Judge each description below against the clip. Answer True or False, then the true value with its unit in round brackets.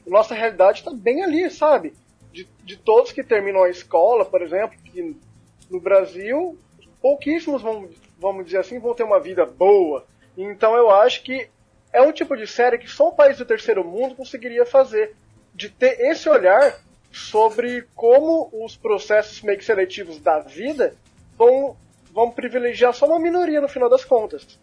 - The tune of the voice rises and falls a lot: True (6.5 semitones)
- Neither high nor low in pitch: False (255 Hz)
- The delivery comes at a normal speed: True (170 wpm)